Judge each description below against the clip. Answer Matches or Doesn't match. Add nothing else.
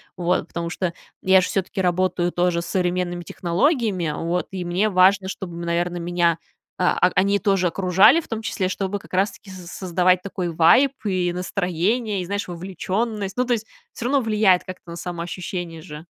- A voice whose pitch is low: Doesn't match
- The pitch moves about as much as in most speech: Doesn't match